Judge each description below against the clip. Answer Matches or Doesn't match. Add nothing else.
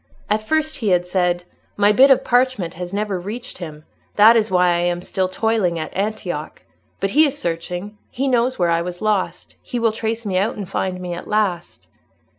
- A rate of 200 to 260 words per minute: Matches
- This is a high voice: Matches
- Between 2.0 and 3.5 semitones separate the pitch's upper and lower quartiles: Doesn't match